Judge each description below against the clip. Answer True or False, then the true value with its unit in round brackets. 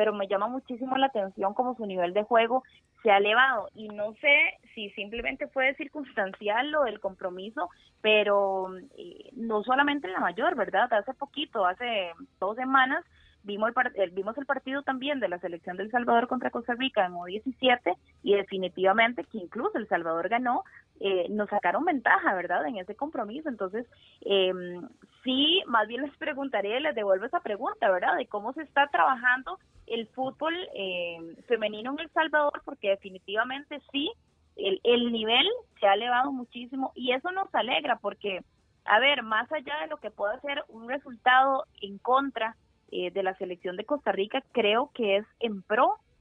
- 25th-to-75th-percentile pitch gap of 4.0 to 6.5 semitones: True (5.5 semitones)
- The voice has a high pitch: True (235 Hz)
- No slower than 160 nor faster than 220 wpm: True (170 wpm)